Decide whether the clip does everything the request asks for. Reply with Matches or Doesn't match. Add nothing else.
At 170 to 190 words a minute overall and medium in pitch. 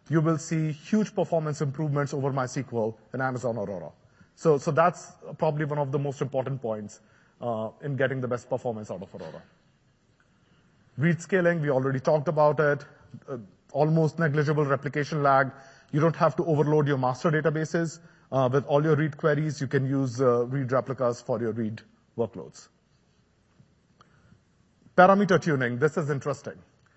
Doesn't match